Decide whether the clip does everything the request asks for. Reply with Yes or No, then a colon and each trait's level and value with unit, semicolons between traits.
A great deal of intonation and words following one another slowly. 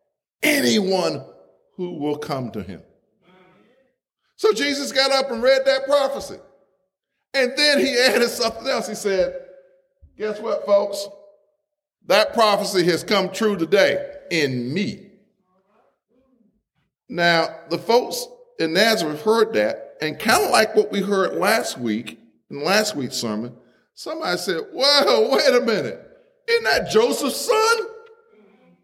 Yes: wide, 6.9 semitones; slow, 130 wpm